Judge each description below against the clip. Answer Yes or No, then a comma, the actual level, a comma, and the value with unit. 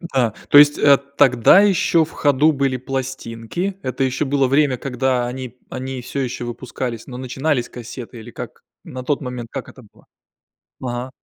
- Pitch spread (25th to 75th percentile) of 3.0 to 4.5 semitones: No, narrow, 2.4 semitones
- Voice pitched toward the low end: Yes, low, 130 Hz